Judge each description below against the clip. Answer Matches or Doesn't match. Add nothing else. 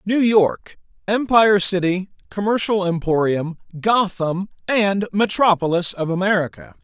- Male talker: Matches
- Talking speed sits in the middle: Doesn't match